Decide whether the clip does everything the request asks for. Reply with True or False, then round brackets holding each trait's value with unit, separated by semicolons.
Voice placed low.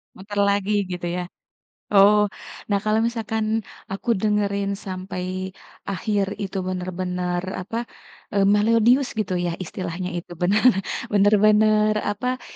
False (200 Hz)